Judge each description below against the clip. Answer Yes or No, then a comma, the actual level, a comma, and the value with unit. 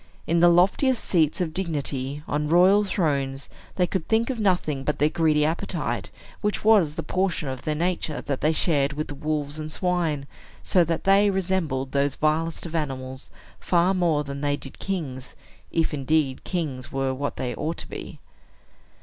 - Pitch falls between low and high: Yes, medium, 155 Hz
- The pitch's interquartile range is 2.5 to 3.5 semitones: No, average, 4.0 semitones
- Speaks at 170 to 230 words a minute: Yes, average, 175 wpm